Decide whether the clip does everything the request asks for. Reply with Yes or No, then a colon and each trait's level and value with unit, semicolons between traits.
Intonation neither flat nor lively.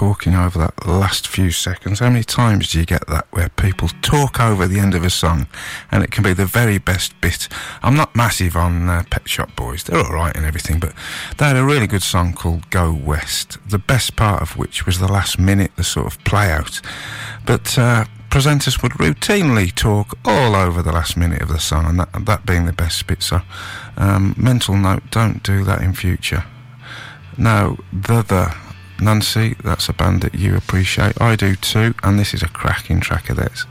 Yes: average, 3.9 semitones